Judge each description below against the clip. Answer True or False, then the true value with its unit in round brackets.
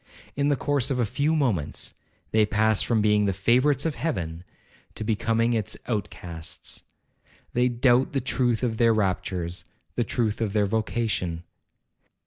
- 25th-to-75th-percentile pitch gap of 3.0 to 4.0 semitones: True (3.7 semitones)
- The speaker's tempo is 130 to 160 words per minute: True (145 wpm)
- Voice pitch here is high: False (110 Hz)